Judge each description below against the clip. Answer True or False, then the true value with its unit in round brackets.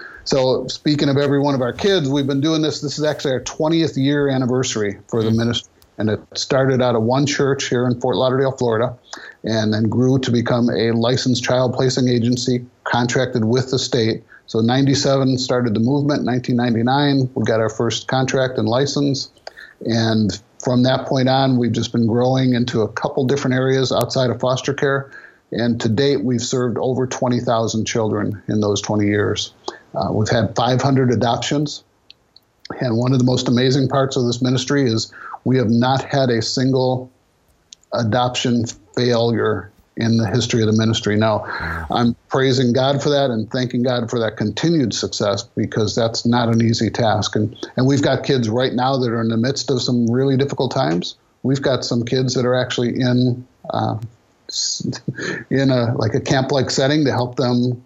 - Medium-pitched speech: False (125 Hz)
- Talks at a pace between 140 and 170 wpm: False (185 wpm)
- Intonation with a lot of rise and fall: False (2.6 semitones)